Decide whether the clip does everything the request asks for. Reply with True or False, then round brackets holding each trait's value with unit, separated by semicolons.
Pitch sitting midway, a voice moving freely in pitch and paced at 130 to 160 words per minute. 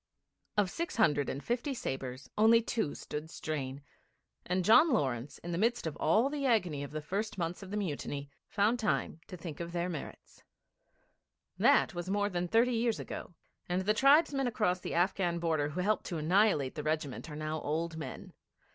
False (175 Hz; 5.9 semitones; 185 wpm)